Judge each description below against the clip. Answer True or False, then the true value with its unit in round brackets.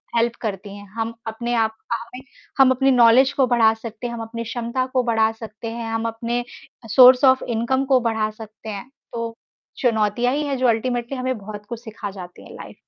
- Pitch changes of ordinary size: False (2.1 semitones)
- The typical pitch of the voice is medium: False (230 Hz)